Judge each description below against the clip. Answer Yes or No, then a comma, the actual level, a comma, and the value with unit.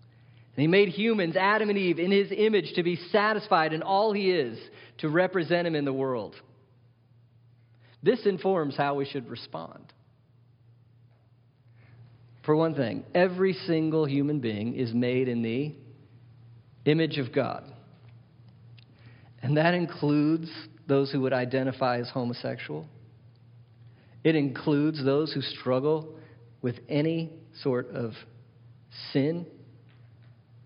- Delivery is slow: Yes, slow, 120 wpm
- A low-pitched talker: Yes, low, 130 Hz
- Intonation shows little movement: No, average, 4.8 semitones